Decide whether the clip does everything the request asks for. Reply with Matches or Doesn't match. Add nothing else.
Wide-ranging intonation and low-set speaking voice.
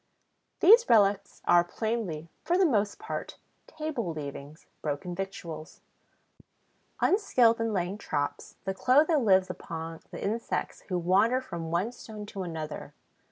Doesn't match